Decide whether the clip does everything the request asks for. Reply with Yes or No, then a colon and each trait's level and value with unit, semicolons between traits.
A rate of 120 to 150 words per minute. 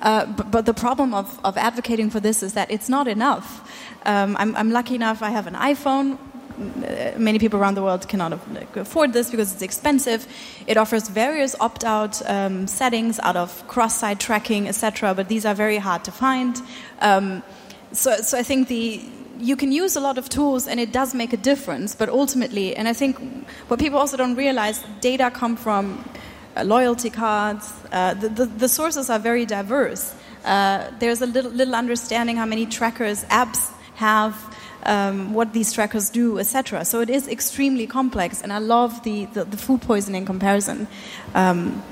No: average, 185 wpm